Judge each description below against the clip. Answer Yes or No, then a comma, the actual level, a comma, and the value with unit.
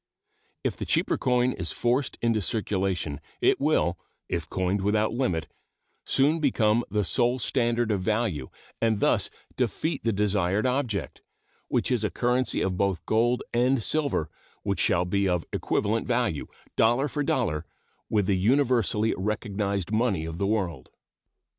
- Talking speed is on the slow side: No, average, 145 wpm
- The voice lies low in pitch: Yes, low, 110 Hz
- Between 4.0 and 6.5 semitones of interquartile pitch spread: Yes, average, 4.3 semitones